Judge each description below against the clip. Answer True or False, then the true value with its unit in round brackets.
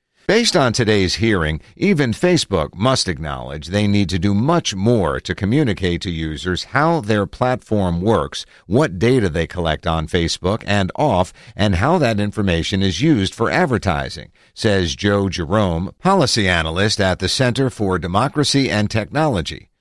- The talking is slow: False (150 wpm)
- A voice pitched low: True (100 Hz)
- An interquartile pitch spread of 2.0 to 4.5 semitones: False (5.3 semitones)